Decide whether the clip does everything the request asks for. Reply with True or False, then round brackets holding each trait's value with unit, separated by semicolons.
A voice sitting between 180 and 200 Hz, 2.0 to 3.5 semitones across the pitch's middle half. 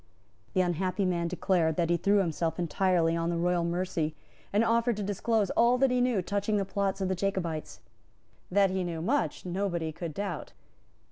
True (185 Hz; 2.9 semitones)